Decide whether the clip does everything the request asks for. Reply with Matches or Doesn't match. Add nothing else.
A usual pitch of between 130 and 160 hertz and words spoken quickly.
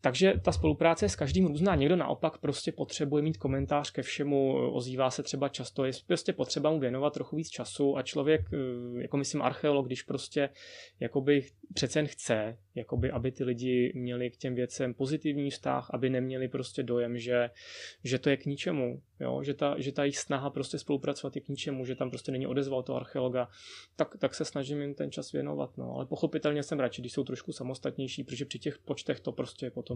Matches